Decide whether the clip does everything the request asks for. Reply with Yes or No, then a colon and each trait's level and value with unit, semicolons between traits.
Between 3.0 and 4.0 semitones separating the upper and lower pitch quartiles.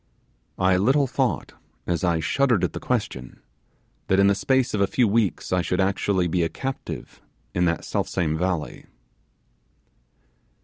No: average, 4.5 semitones